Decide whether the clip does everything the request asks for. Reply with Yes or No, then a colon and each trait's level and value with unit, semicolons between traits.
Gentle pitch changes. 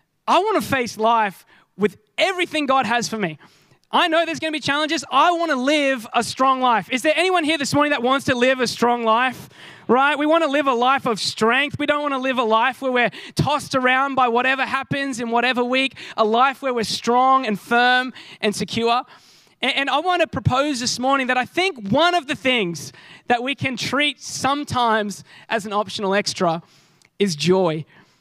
No: average, 4.0 semitones